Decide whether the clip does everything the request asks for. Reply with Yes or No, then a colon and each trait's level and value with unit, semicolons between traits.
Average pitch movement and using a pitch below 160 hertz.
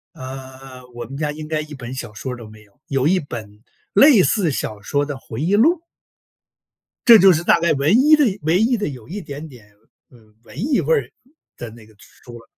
No: wide, 6.5 semitones; medium, 140 Hz